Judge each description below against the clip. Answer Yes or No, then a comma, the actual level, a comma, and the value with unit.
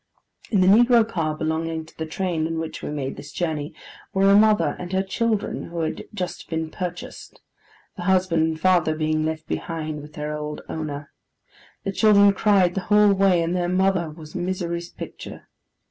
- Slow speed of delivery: No, average, 180 wpm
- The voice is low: No, medium, 170 Hz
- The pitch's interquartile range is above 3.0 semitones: Yes, average, 3.4 semitones